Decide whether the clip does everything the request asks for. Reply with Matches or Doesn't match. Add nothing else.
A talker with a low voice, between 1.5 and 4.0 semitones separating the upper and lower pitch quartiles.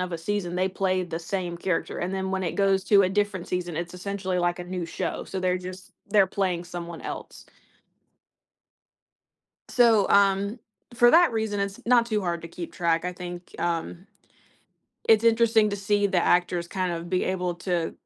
Doesn't match